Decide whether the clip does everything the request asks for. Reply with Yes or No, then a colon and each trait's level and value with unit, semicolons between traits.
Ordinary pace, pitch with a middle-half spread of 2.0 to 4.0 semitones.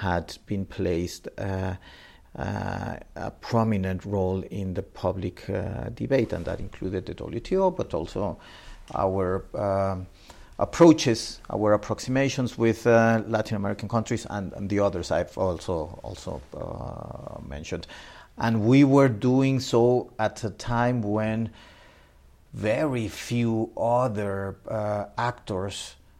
No: slow, 120 wpm; average, 3.6 semitones